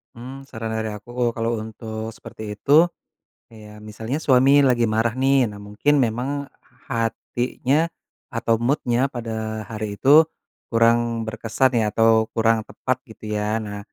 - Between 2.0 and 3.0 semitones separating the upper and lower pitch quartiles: Yes, narrow, 2.6 semitones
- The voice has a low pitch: Yes, low, 115 Hz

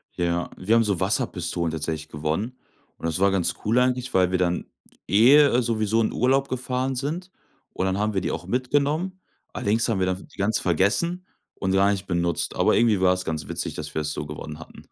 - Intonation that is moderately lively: No, wide, 6.3 semitones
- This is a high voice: No, low, 100 Hz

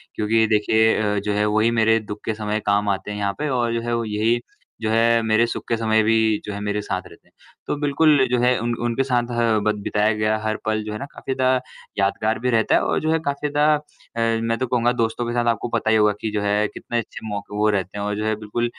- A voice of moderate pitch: No, low, 110 Hz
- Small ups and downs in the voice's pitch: Yes, narrow, 2.2 semitones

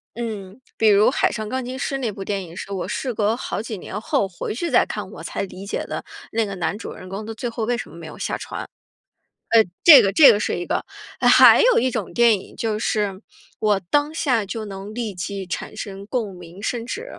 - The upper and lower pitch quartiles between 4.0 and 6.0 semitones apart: No, average, 3.4 semitones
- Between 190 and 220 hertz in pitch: Yes, high, 215 Hz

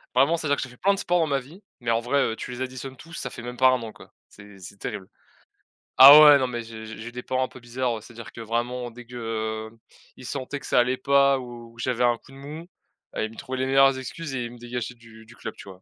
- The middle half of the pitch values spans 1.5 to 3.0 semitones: Yes, average, 2.7 semitones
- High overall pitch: No, low, 125 Hz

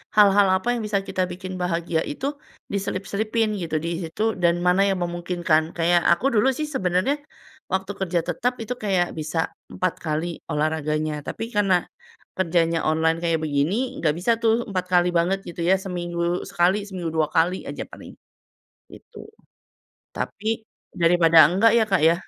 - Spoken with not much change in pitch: No, average, 3.1 semitones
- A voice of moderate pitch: Yes, medium, 180 Hz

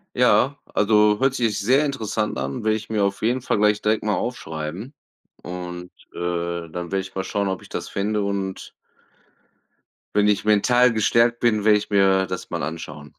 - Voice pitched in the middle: No, low, 105 Hz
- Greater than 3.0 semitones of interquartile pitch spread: No, narrow, 2.6 semitones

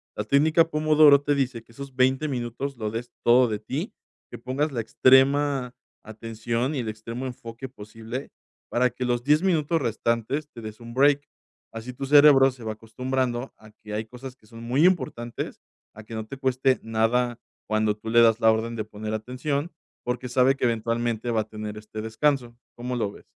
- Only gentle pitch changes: No, average, 3.3 semitones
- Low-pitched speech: Yes, low, 120 Hz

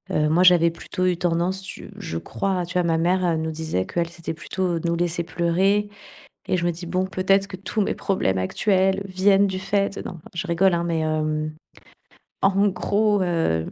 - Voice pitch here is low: No, medium, 175 Hz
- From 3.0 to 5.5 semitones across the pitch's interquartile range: No, narrow, 2.4 semitones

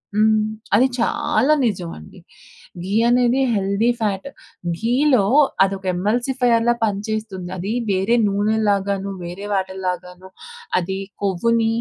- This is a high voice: Yes, high, 205 Hz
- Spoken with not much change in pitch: No, average, 3.3 semitones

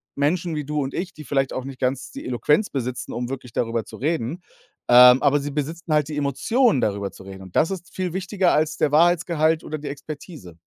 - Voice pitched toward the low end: No, medium, 145 Hz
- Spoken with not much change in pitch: No, average, 4.4 semitones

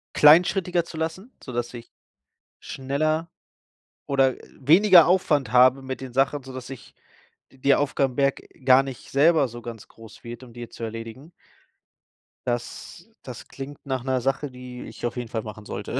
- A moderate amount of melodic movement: Yes, average, 3.2 semitones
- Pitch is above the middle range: No, low, 135 Hz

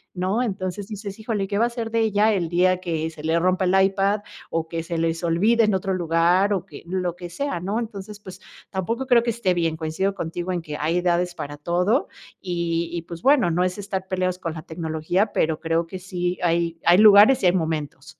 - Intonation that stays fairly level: No, average, 3.2 semitones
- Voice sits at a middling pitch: Yes, medium, 180 Hz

